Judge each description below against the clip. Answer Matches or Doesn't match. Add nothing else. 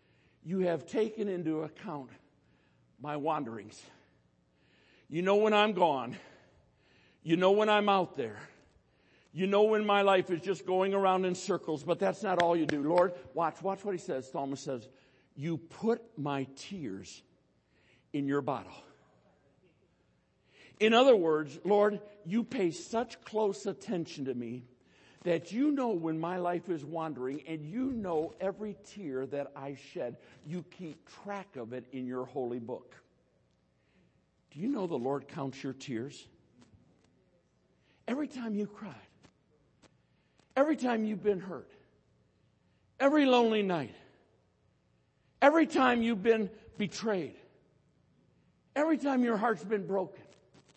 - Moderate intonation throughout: Doesn't match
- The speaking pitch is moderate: Matches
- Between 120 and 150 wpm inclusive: Matches